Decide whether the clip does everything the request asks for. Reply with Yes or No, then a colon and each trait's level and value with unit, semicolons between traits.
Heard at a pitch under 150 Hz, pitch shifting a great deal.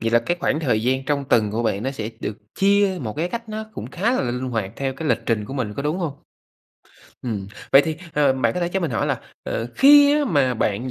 Yes: low, 135 Hz; wide, 7.0 semitones